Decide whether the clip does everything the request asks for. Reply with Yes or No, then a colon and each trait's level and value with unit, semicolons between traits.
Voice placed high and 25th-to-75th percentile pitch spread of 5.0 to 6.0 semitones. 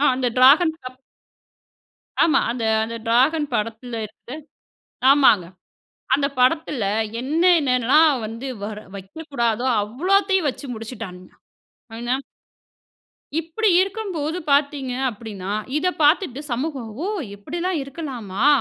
Yes: very high, 265 Hz; wide, 5.5 semitones